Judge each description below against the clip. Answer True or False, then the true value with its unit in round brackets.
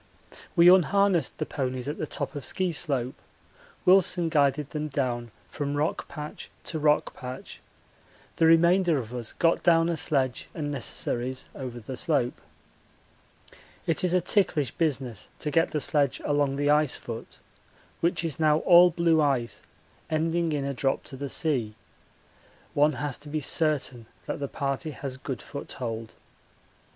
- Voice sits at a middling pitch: True (145 Hz)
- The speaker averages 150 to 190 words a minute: True (155 wpm)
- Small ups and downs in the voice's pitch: False (3.8 semitones)